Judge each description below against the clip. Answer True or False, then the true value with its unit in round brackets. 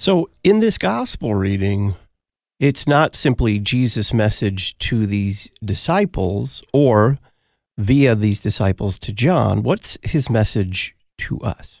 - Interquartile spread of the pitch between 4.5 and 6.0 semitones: True (5.6 semitones)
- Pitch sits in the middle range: False (110 Hz)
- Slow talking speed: True (120 wpm)